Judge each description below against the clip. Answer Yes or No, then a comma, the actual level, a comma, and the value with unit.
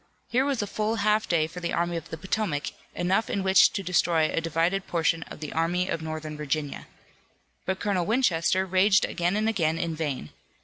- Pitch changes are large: No, average, 3.5 semitones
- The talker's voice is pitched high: No, medium, 175 Hz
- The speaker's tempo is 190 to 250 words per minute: Yes, average, 195 wpm